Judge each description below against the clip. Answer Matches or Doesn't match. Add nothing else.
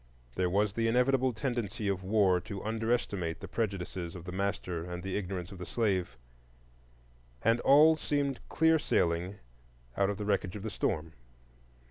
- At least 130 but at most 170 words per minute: Matches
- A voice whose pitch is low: Matches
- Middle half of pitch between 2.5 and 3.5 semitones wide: Doesn't match